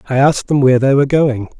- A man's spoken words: Yes, male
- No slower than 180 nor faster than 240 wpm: No, fast, 265 wpm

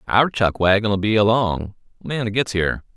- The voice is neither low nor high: No, low, 105 Hz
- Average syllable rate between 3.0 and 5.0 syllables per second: Yes, 4.9 syllables/s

